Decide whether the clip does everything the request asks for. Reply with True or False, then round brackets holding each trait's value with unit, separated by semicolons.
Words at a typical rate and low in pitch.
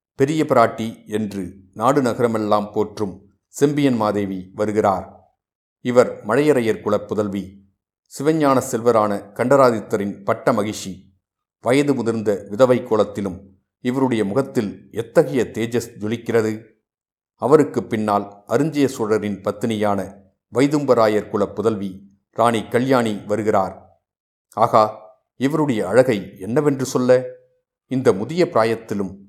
True (95 wpm; 110 Hz)